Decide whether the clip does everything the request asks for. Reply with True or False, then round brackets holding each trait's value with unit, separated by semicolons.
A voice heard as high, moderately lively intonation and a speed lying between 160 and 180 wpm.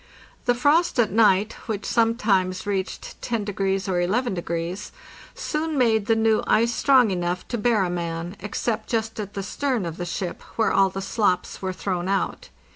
True (210 Hz; 4.0 semitones; 175 wpm)